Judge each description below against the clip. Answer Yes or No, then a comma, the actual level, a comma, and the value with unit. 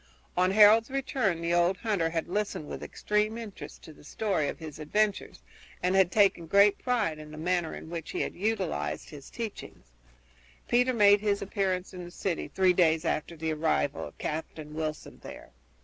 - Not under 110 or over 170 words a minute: No, average, 180 wpm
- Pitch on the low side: No, medium, 180 Hz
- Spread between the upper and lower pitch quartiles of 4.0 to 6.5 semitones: Yes, average, 4.6 semitones